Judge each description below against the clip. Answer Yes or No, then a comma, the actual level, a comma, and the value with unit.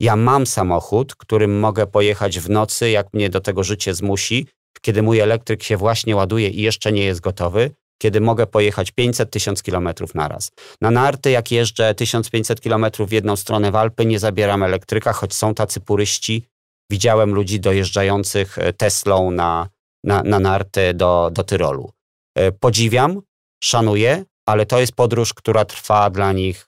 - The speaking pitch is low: Yes, low, 105 Hz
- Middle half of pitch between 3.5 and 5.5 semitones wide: No, narrow, 2.4 semitones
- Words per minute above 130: Yes, fast, 160 wpm